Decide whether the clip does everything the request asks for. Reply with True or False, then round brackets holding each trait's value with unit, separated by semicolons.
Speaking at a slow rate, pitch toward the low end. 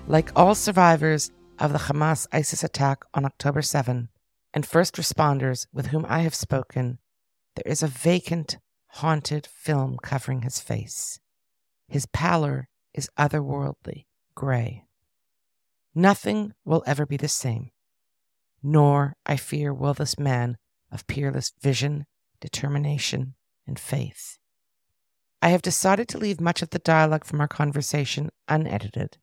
False (130 wpm; 145 Hz)